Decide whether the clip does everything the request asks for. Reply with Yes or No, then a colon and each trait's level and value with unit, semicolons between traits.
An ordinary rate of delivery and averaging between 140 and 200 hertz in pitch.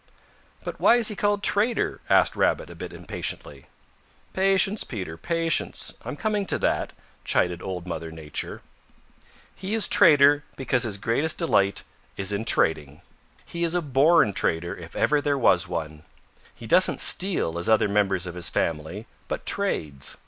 No: average, 155 wpm; low, 110 Hz